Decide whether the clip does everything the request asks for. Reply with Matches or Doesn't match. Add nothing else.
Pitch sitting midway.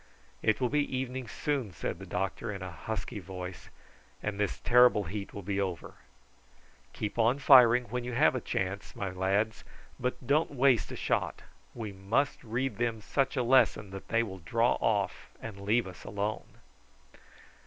Doesn't match